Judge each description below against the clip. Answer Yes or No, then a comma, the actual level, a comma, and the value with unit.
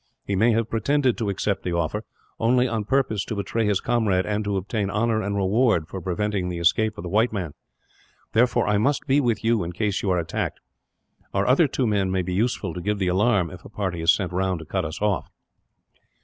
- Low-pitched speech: Yes, low, 105 Hz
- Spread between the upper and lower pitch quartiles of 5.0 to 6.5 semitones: No, average, 3.5 semitones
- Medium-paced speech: No, fast, 225 wpm